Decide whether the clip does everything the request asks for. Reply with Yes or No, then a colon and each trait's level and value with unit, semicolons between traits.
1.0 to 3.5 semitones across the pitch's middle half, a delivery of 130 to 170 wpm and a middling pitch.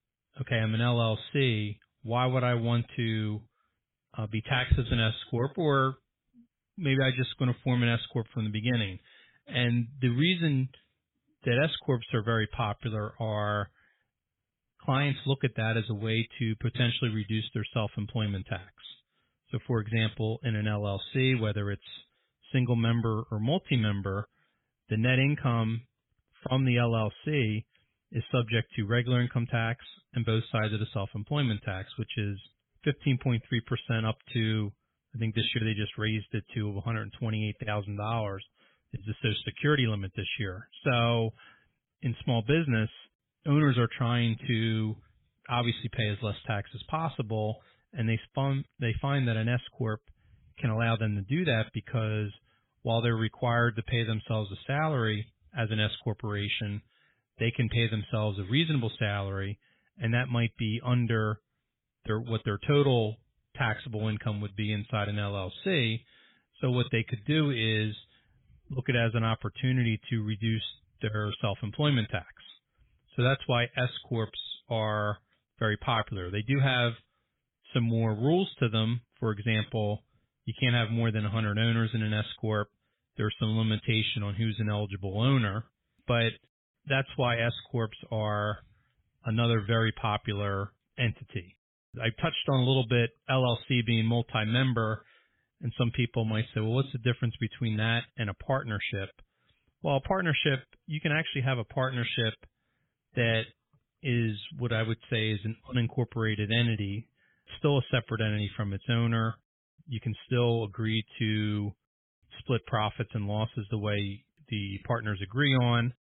No: narrow, 2.5 semitones; average, 155 wpm; low, 115 Hz